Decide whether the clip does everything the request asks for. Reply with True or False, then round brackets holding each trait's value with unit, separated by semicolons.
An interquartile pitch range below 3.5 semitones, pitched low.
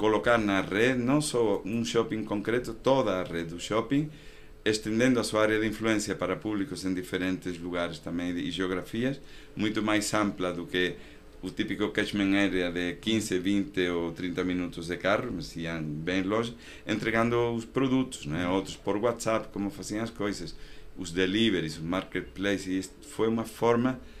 False (3.8 semitones; 100 Hz)